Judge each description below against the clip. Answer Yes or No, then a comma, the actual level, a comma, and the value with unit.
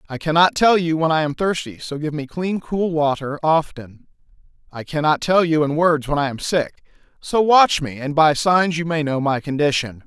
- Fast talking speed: Yes, fast, 215 wpm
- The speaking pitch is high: No, medium, 155 Hz